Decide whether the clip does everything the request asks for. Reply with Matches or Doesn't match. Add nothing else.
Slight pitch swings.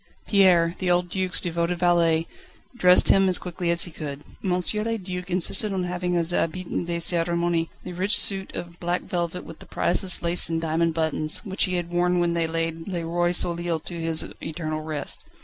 Matches